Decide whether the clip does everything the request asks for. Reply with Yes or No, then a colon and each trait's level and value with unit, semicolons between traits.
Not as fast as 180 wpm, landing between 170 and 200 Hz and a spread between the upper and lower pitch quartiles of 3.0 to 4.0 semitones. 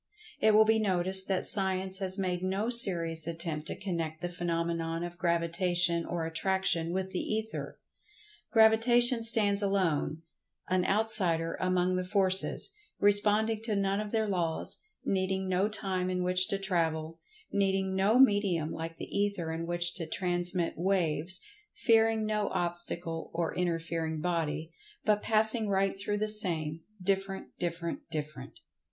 Yes: slow, 135 wpm; medium, 185 Hz; average, 3.5 semitones